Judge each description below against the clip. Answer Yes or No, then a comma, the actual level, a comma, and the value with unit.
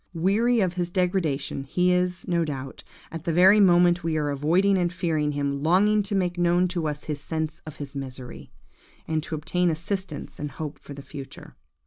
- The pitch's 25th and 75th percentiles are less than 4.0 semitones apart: Yes, average, 3.5 semitones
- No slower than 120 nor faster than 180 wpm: No, average, 190 wpm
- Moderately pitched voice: Yes, medium, 170 Hz